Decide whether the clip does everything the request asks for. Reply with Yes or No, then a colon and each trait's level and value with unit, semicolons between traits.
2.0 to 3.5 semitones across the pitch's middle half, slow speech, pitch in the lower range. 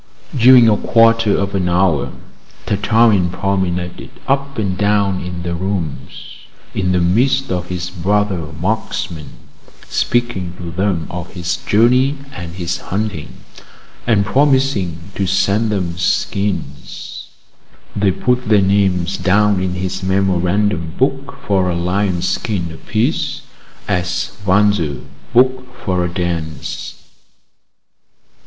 Yes: average, 3.1 semitones; slow, 115 wpm; very low, 95 Hz